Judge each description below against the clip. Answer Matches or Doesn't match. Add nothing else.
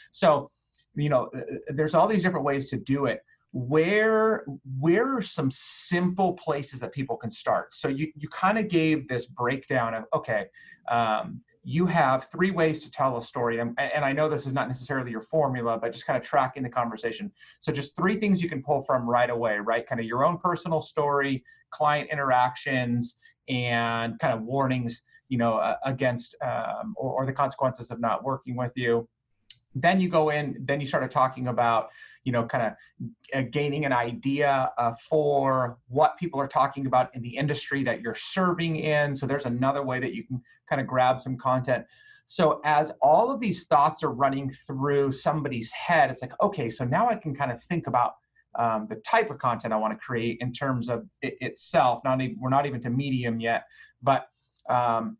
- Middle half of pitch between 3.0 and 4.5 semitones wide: Matches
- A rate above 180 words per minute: Matches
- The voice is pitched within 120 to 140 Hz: Matches